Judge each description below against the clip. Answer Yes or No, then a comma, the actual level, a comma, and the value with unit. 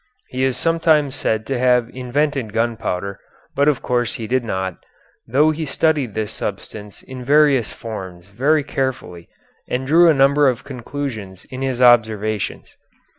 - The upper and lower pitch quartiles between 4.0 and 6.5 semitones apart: Yes, average, 4.4 semitones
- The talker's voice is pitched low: Yes, low, 125 Hz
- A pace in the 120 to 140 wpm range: No, average, 150 wpm